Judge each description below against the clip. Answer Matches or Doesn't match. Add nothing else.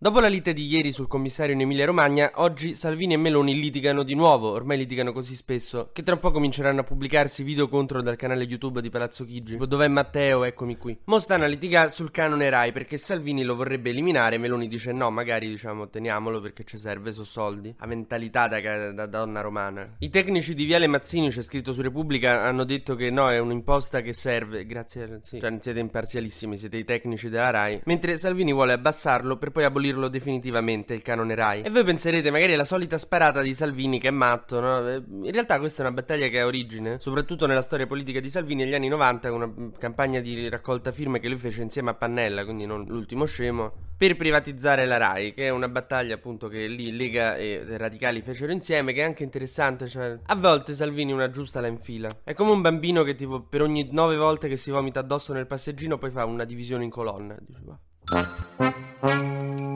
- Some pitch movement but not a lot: Matches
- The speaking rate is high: Matches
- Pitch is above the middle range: Doesn't match